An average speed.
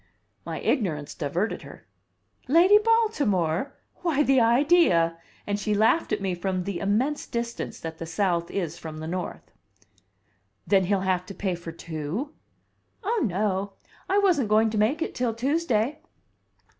Yes: average, 150 wpm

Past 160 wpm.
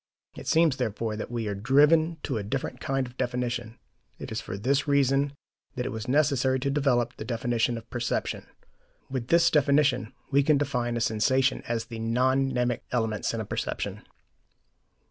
Yes: average, 175 wpm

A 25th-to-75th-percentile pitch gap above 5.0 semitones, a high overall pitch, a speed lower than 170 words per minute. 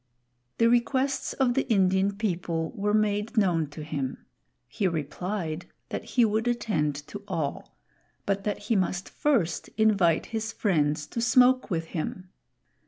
Yes: wide, 5.5 semitones; high, 200 Hz; average, 145 wpm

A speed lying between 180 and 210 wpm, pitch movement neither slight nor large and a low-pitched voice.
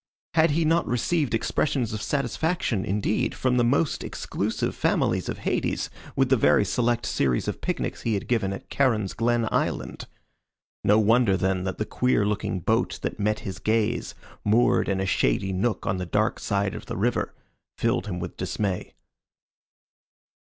No: average, 165 wpm; average, 4.1 semitones; low, 110 Hz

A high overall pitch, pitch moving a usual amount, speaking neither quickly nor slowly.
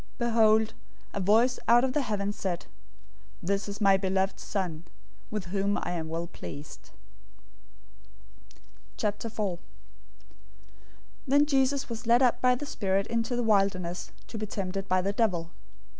Yes: high, 205 Hz; average, 3.6 semitones; average, 145 wpm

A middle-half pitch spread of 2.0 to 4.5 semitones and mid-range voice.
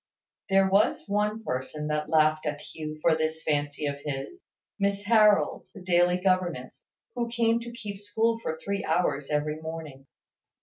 No: average, 5.2 semitones; medium, 175 Hz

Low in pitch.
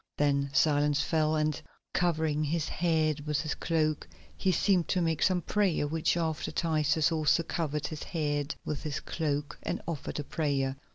No: medium, 155 Hz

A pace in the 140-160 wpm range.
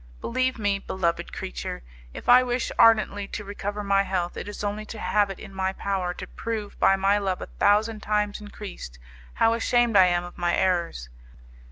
No: average, 190 wpm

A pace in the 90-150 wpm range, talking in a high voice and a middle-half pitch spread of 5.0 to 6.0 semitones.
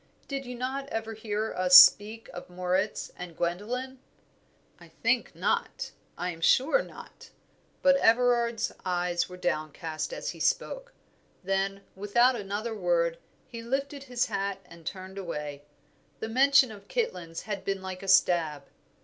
Yes: average, 145 wpm; high, 200 Hz; wide, 5.6 semitones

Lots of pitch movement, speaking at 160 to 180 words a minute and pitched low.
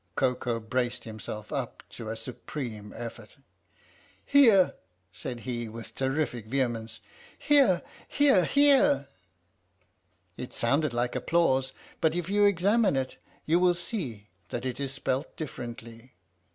No: wide, 6.5 semitones; average, 140 wpm; low, 130 Hz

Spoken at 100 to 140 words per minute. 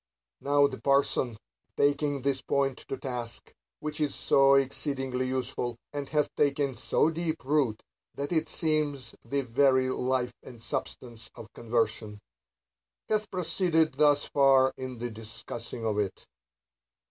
Yes: slow, 135 wpm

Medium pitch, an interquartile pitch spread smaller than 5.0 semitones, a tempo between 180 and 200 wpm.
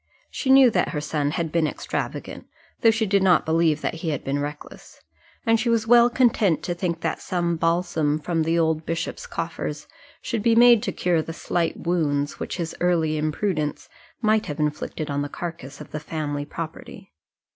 Yes: medium, 165 Hz; average, 3.8 semitones; average, 190 wpm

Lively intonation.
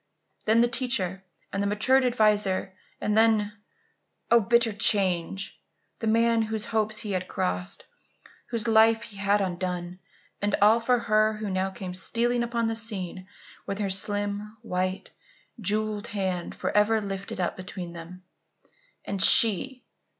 No: average, 3.0 semitones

